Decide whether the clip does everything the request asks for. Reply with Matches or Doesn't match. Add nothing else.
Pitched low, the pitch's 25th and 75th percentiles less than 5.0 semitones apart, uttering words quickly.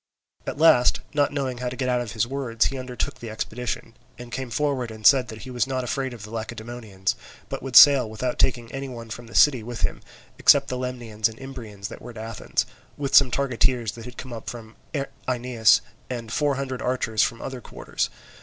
Matches